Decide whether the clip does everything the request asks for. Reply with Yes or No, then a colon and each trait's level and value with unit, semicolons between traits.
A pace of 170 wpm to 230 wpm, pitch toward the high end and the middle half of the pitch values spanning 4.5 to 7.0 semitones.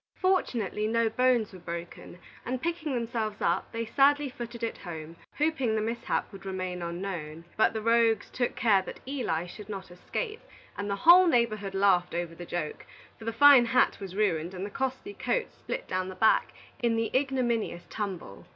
Yes: average, 180 wpm; high, 220 Hz; average, 5.3 semitones